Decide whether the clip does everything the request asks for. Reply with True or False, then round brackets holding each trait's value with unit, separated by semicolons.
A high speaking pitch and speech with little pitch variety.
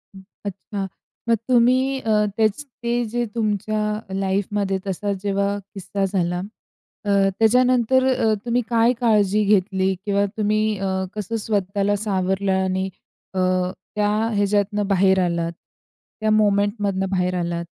True (205 Hz; 2.2 semitones)